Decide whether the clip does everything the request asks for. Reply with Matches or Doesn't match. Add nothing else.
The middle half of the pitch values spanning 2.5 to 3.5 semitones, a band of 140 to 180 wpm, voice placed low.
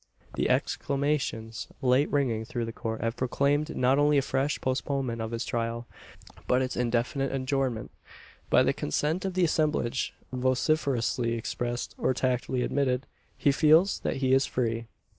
Matches